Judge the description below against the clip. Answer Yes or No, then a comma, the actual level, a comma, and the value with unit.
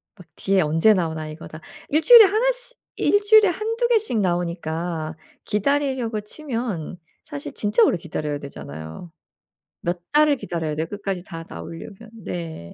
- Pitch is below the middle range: No, medium, 185 Hz